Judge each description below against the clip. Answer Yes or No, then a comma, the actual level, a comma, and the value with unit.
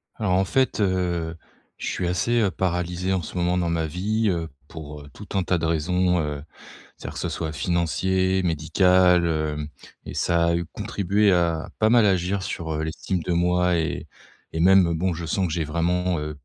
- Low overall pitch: Yes, very low, 90 Hz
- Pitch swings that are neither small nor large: No, narrow, 2.3 semitones